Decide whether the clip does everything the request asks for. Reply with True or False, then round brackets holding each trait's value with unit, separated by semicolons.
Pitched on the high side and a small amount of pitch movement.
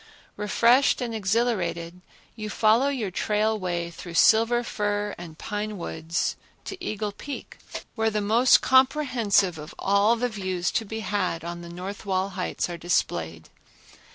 False (205 Hz; 4.0 semitones)